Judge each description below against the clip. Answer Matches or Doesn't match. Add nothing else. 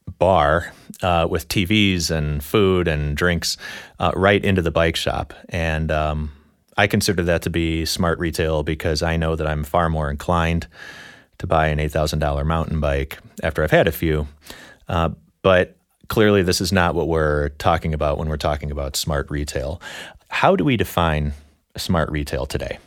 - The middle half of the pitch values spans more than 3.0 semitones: Doesn't match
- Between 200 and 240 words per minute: Doesn't match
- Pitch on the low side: Matches